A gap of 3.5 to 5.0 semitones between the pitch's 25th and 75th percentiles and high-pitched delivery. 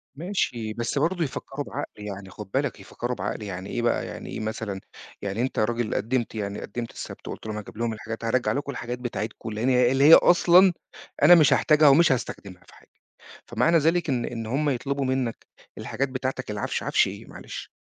No: average, 4.2 semitones; low, 120 Hz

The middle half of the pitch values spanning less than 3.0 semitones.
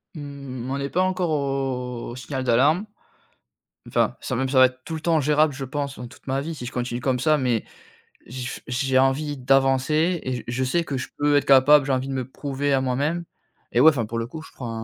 Yes: narrow, 2.4 semitones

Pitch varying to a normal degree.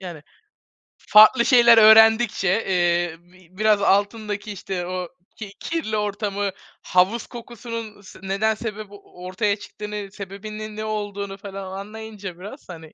No: narrow, 2.2 semitones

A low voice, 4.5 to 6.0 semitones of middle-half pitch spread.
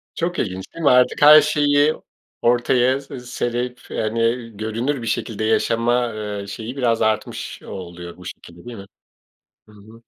No: low, 115 Hz; average, 2.8 semitones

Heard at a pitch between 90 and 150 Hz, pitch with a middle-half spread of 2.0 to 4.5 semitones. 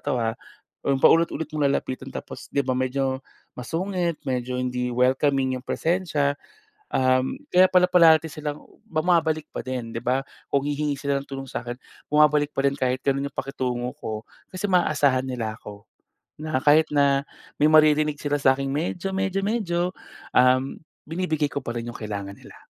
Yes: medium, 140 Hz; average, 3.4 semitones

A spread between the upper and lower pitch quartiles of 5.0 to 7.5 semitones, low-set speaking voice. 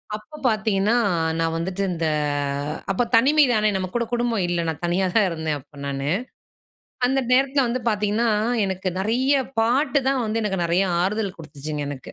No: wide, 5.5 semitones; high, 205 Hz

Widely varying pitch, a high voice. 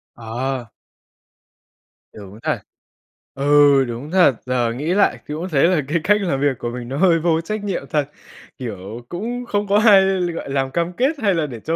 No: wide, 6.3 semitones; medium, 150 Hz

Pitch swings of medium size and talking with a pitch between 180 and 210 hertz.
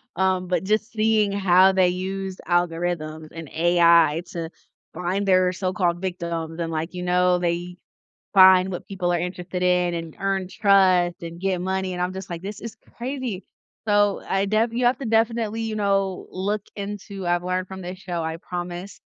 No: narrow, 2.1 semitones; medium, 185 Hz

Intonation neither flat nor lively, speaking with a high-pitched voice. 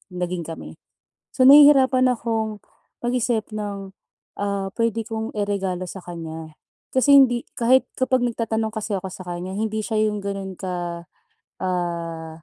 Yes: average, 4.2 semitones; high, 205 Hz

